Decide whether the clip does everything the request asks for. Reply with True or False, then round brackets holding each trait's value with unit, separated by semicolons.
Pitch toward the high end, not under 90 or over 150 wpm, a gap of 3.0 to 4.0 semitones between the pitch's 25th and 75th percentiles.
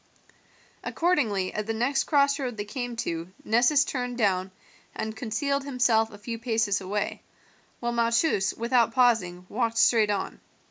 True (230 Hz; 140 wpm; 3.3 semitones)